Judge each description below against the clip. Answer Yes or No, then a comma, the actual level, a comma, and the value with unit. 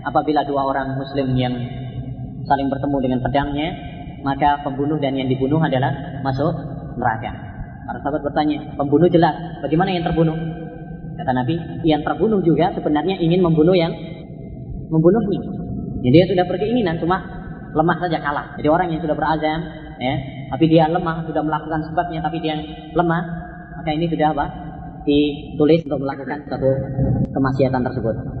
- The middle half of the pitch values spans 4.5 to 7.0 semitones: No, average, 2.9 semitones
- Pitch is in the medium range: Yes, medium, 150 Hz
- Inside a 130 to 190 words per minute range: Yes, average, 145 wpm